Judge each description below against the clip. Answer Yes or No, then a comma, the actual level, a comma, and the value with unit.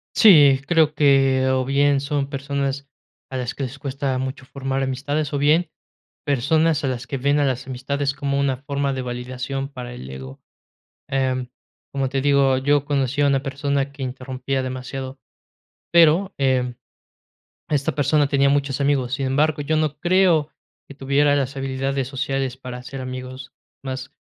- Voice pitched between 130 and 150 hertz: Yes, low, 135 Hz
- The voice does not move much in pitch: Yes, narrow, 1.5 semitones